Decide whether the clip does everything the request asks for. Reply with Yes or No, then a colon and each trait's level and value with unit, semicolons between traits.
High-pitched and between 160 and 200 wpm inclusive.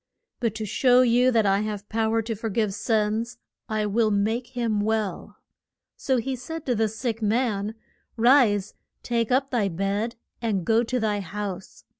Yes: high, 220 Hz; average, 175 wpm